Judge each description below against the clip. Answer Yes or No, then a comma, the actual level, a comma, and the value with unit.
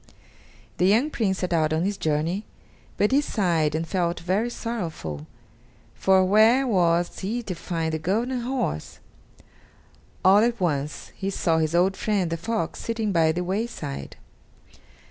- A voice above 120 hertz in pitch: Yes, medium, 185 Hz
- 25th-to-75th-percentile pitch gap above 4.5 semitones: Yes, average, 5.0 semitones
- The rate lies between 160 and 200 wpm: No, average, 150 wpm